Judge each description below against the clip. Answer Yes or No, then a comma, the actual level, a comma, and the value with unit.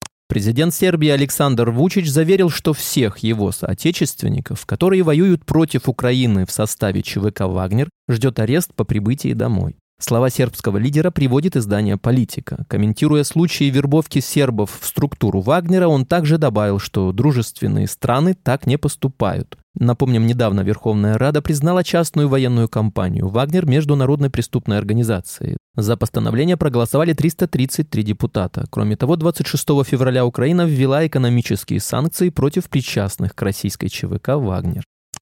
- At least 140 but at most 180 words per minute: No, average, 130 wpm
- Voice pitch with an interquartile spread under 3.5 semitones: No, wide, 5.5 semitones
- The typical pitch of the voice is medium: No, low, 130 Hz